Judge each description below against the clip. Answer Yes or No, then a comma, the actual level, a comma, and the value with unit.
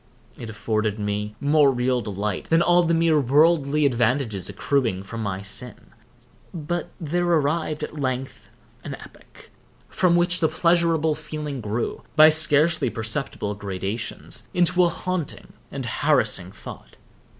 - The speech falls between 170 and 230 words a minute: No, slow, 135 wpm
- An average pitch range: No, wide, 6.8 semitones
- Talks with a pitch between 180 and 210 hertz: No, medium, 140 Hz